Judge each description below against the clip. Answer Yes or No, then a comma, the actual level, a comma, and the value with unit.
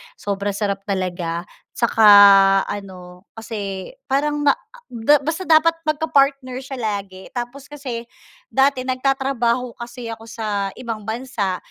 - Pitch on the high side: Yes, high, 235 Hz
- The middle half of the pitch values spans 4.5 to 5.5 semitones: Yes, average, 5.2 semitones